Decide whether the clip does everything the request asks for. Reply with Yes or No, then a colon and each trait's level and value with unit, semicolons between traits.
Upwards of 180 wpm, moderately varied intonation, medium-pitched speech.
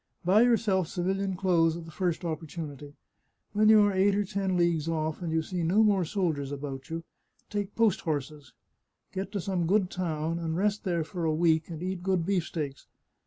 Yes: average, 190 wpm; average, 3.3 semitones; medium, 175 Hz